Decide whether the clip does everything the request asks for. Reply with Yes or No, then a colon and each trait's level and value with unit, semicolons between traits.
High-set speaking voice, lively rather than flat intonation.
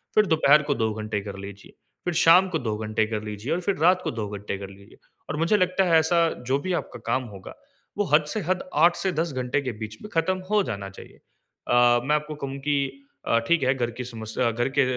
No: low, 135 Hz; wide, 7.6 semitones